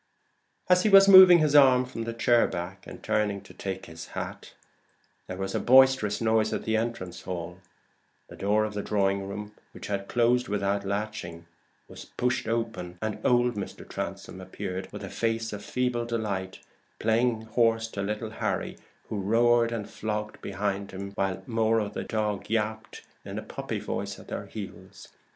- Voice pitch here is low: Yes, low, 110 Hz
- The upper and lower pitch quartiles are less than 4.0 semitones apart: Yes, average, 2.9 semitones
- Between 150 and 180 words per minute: Yes, average, 170 wpm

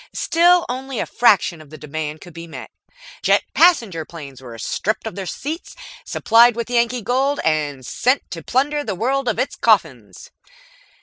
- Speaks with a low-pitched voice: No, high, 220 Hz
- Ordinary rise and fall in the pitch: No, wide, 8.6 semitones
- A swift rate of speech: No, average, 170 wpm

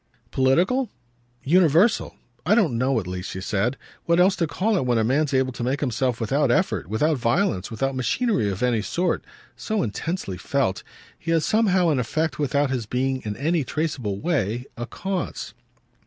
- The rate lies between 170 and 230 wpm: Yes, average, 175 wpm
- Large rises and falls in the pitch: Yes, wide, 6.2 semitones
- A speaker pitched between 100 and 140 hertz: Yes, low, 135 Hz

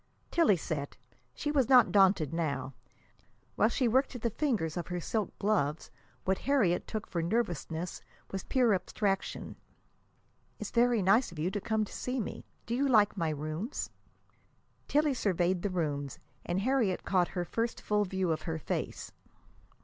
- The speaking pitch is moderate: No, high, 195 Hz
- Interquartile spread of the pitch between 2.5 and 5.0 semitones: No, wide, 5.5 semitones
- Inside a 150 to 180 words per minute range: Yes, average, 165 wpm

